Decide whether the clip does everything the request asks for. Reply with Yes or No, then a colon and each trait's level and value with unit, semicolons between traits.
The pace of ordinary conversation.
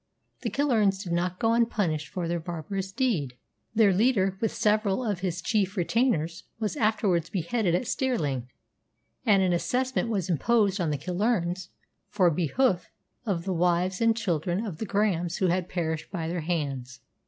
Yes: average, 165 wpm